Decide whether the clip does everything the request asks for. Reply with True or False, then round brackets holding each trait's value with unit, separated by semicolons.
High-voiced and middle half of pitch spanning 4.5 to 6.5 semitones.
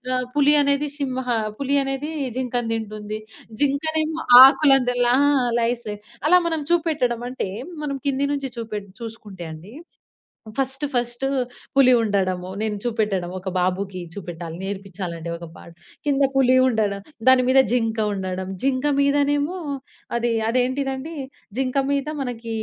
True (245 Hz; 5.1 semitones)